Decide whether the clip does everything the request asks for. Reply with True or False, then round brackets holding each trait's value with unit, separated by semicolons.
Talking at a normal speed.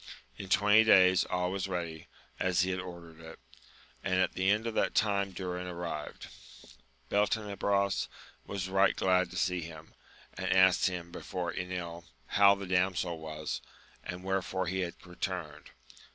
True (150 wpm)